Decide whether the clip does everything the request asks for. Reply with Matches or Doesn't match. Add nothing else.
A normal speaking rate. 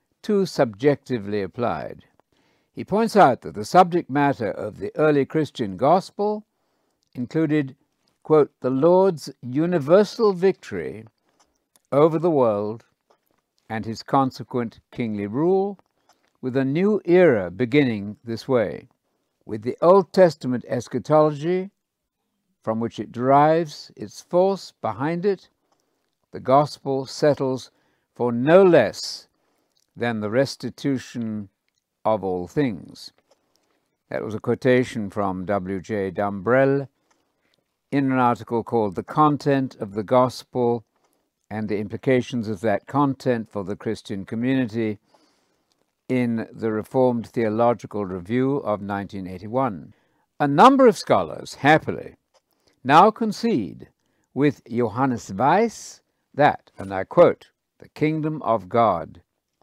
Doesn't match